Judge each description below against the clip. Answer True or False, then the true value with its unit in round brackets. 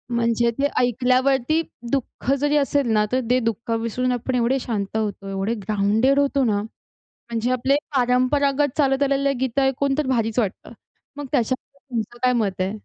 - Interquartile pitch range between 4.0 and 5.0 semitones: False (3.3 semitones)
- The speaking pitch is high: True (250 Hz)